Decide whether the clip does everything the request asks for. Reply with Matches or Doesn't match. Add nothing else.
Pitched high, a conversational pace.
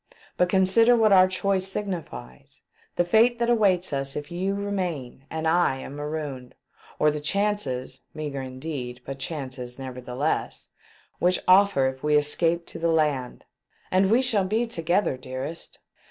Doesn't match